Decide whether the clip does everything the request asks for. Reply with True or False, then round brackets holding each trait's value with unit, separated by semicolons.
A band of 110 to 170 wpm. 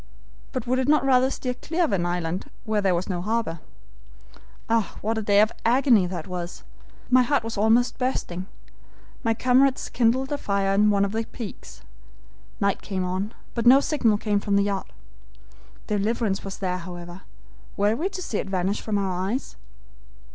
False (180 wpm)